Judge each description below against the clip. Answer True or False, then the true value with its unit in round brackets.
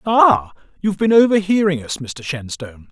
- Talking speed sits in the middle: True (145 wpm)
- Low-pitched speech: False (160 Hz)